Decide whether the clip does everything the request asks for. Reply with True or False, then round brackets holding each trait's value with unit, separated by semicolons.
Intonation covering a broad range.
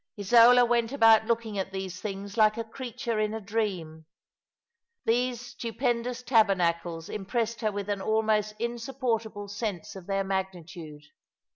False (3.3 semitones)